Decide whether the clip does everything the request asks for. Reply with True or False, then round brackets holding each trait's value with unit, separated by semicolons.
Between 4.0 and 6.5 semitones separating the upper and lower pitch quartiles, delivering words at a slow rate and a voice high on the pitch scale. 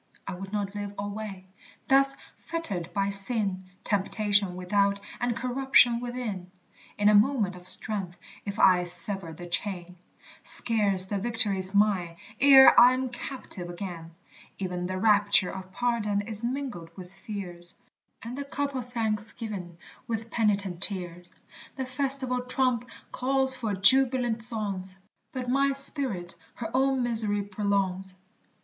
True (4.6 semitones; 130 wpm; 205 Hz)